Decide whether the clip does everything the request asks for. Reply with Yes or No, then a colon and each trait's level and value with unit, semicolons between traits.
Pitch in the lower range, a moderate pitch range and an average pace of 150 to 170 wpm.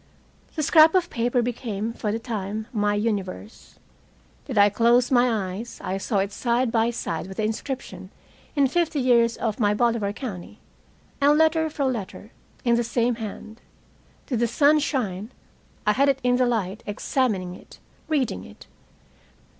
No: high, 230 Hz; average, 3.8 semitones; average, 160 wpm